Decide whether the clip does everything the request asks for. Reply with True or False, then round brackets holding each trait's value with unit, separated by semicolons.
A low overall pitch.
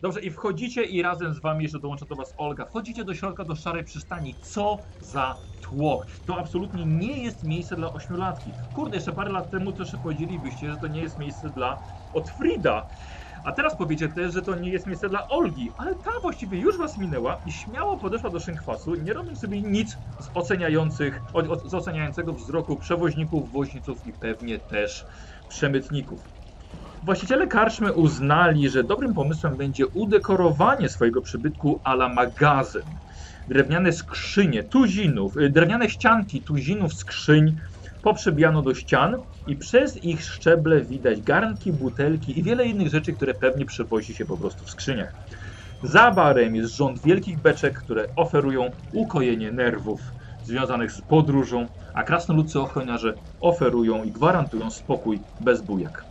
False (155 Hz)